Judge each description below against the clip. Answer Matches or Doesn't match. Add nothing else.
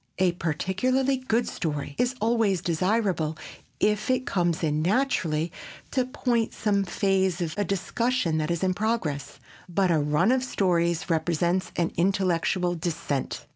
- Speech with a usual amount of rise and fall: Matches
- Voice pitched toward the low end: Doesn't match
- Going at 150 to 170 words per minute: Doesn't match